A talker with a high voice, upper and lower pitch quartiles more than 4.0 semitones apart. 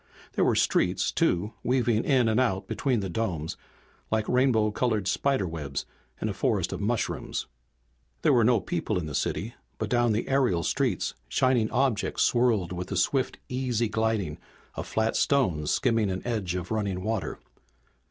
No: low, 110 Hz; average, 4.9 semitones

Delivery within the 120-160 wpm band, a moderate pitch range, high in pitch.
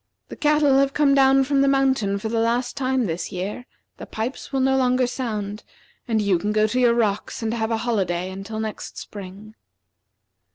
No: average, 195 wpm; average, 4.2 semitones; high, 230 Hz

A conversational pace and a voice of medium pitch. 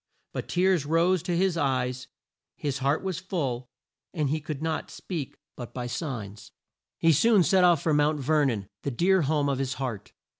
Yes: average, 185 wpm; medium, 150 Hz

